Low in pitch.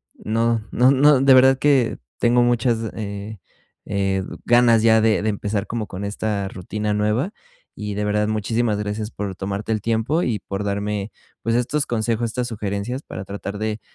Yes: low, 110 Hz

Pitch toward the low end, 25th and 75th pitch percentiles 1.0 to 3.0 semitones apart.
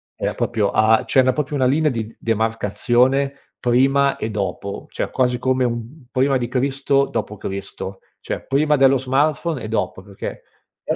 No: low, 130 Hz; average, 3.5 semitones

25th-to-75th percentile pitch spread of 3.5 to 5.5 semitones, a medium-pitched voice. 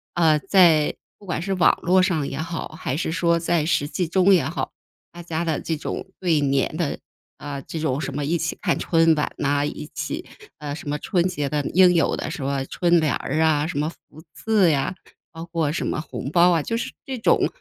No: average, 2.8 semitones; medium, 160 Hz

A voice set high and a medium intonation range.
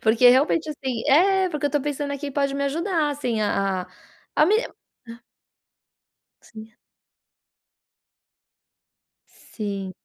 Yes: very high, 280 Hz; average, 5.0 semitones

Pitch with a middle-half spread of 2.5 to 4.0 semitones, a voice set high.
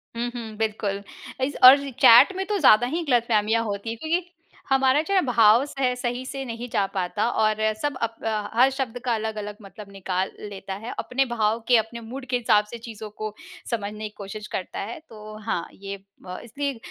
Yes: average, 3.3 semitones; high, 225 Hz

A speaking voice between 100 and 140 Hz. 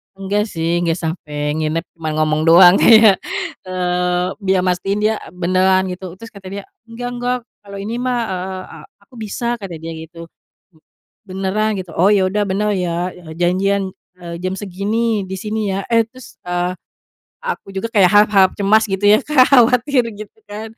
No: high, 195 Hz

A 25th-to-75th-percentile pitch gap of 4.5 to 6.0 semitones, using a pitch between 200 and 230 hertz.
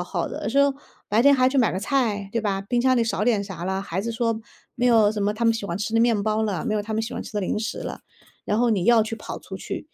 No: narrow, 2.6 semitones; high, 220 Hz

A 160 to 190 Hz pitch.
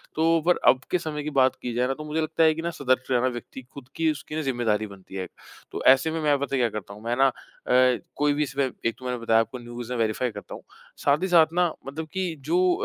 No: low, 135 Hz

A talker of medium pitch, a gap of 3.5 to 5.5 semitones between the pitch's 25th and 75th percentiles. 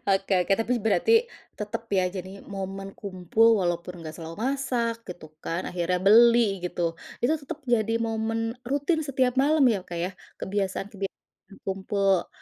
No: high, 200 Hz; average, 4.1 semitones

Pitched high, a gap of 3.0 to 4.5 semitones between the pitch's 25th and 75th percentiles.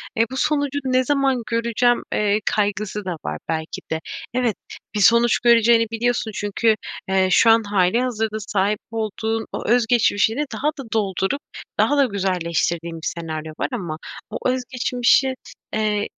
Yes: high, 225 Hz; average, 3.8 semitones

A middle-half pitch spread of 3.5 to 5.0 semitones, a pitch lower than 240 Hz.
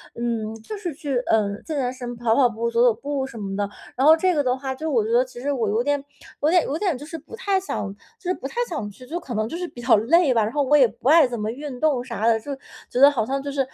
No: average, 4.2 semitones; very high, 260 Hz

